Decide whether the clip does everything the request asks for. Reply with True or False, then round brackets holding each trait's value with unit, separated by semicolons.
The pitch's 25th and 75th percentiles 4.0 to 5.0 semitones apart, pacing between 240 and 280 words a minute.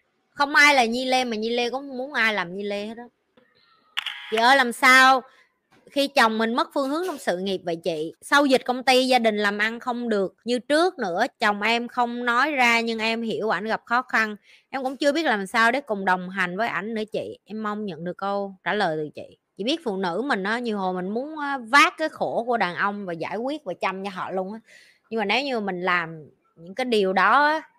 True (4.7 semitones; 250 wpm)